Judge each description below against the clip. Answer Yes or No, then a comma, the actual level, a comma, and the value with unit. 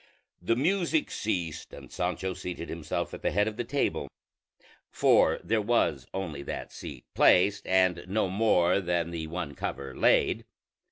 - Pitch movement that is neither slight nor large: Yes, average, 4.2 semitones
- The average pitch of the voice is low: Yes, very low, 90 Hz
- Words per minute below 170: Yes, average, 155 wpm